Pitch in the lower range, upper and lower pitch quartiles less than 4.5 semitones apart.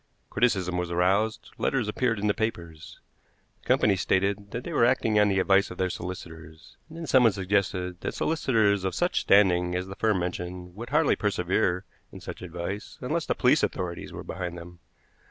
Yes: very low, 95 Hz; average, 3.3 semitones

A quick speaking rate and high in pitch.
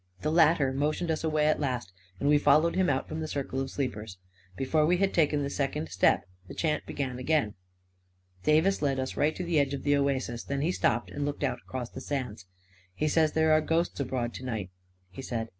No: fast, 225 wpm; medium, 140 Hz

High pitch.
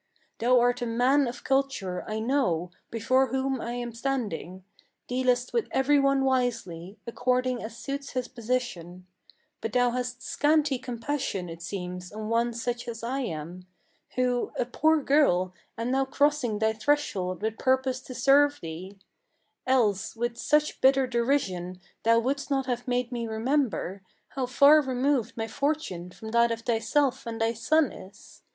Yes: high, 245 Hz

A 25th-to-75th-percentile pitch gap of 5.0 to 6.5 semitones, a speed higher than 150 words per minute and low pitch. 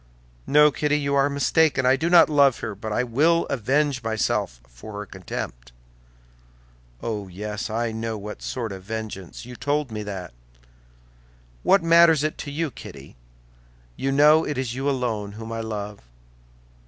Yes: wide, 5.4 semitones; average, 160 wpm; low, 120 Hz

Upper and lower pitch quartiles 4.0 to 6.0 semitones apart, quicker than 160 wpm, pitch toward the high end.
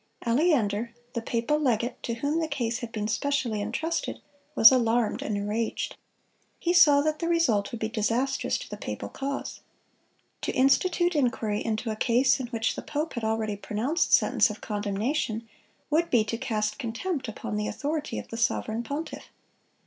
Yes: average, 4.6 semitones; average, 170 wpm; high, 235 Hz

